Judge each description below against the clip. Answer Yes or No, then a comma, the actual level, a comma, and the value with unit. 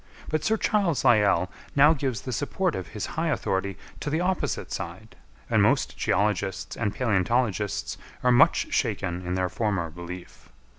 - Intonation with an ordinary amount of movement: No, wide, 7.7 semitones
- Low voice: Yes, low, 105 Hz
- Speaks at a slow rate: No, average, 155 wpm